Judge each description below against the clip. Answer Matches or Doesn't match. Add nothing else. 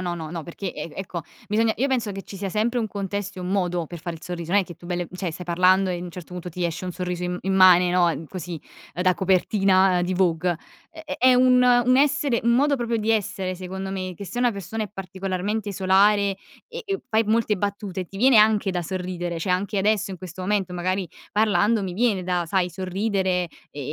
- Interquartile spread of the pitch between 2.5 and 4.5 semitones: Matches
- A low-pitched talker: Doesn't match